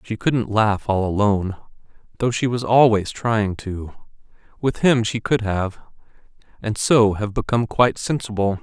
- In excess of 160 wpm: No, average, 155 wpm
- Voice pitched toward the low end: Yes, low, 110 Hz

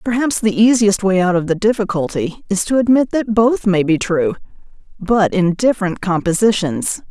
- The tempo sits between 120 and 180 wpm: Yes, average, 160 wpm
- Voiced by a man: No, female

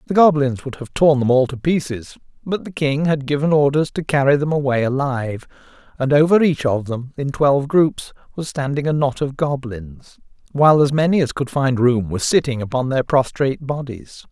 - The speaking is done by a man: Yes, male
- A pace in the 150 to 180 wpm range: No, average, 195 wpm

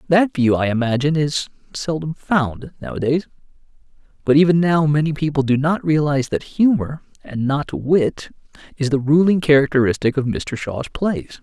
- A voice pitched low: No, medium, 150 Hz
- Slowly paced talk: No, average, 150 wpm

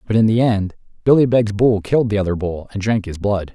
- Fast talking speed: Yes, fast, 255 wpm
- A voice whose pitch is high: No, low, 105 Hz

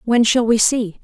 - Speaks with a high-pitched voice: Yes, high, 230 Hz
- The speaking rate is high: Yes, fast, 235 wpm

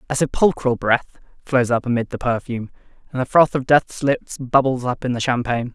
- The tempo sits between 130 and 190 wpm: No, average, 200 wpm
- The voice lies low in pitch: Yes, low, 125 Hz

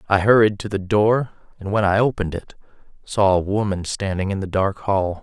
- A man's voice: Yes, male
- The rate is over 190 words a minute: Yes, fast, 205 wpm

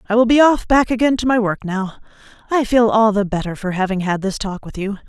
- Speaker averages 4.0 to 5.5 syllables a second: No, 6.0 syllables/s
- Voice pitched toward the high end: Yes, high, 215 Hz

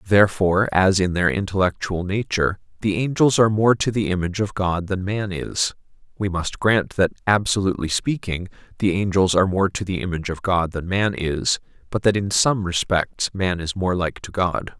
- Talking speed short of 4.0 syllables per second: No, 5.3 syllables/s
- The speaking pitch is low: Yes, very low, 95 Hz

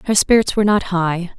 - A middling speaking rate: No, fast, 215 wpm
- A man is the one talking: No, female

